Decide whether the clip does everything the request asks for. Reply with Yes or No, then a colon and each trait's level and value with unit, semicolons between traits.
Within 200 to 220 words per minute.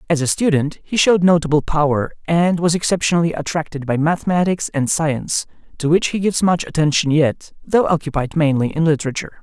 No: average, 170 wpm